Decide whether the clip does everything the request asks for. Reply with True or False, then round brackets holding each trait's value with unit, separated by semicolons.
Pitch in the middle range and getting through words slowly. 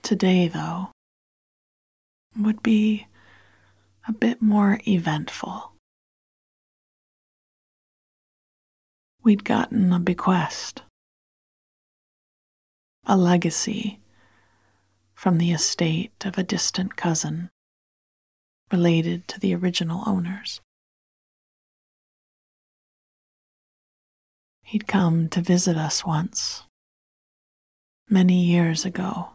True (180 Hz; 70 wpm)